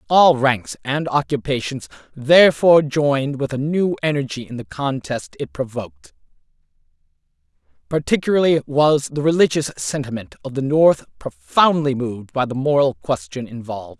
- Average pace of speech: No, slow, 130 wpm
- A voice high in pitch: No, medium, 140 Hz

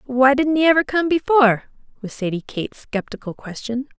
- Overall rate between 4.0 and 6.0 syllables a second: Yes, 5.6 syllables/s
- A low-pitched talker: No, very high, 260 Hz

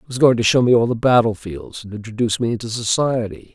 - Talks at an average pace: No, fast, 255 wpm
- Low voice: Yes, low, 115 Hz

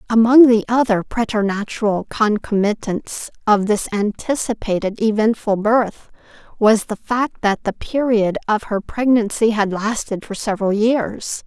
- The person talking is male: No, female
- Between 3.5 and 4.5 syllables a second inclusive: Yes, 4.3 syllables/s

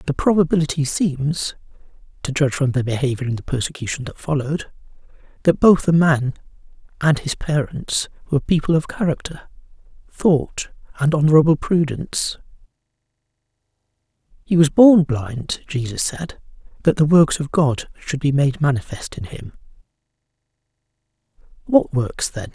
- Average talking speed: No, slow, 130 wpm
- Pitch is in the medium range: Yes, medium, 150 Hz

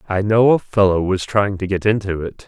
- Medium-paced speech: No, fast, 245 wpm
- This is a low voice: Yes, low, 100 Hz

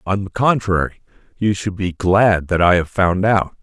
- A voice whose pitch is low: Yes, very low, 95 Hz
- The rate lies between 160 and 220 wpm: Yes, average, 200 wpm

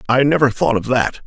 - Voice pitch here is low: Yes, low, 120 Hz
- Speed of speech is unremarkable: No, fast, 240 wpm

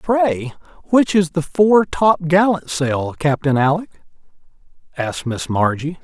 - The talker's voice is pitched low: No, medium, 165 Hz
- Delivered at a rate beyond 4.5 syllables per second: No, 4.0 syllables/s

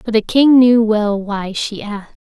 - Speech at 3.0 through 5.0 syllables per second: Yes, 4.4 syllables/s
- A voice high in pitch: Yes, high, 220 Hz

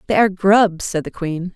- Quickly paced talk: Yes, fast, 230 wpm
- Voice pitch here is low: No, high, 190 Hz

